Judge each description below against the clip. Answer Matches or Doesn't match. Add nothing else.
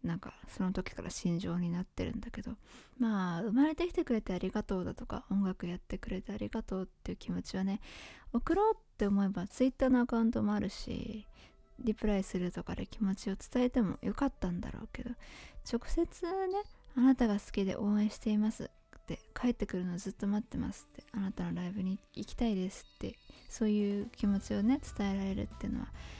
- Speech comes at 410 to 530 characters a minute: Matches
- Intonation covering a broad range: Doesn't match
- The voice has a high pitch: Matches